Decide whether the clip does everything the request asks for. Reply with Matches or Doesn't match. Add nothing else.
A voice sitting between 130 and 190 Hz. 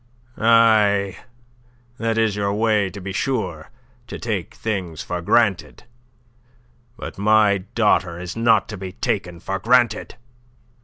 Doesn't match